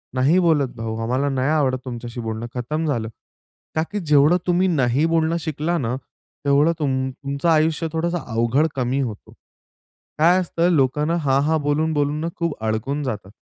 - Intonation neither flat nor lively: Yes, average, 4.0 semitones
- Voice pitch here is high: No, medium, 145 Hz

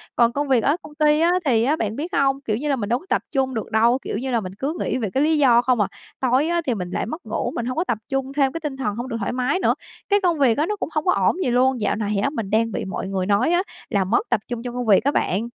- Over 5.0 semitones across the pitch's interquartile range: No, average, 4.5 semitones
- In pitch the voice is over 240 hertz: Yes, very high, 255 Hz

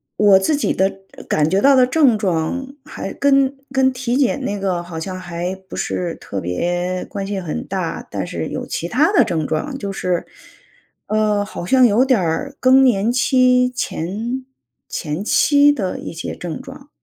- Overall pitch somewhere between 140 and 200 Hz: No, high, 210 Hz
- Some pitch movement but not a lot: No, wide, 6.8 semitones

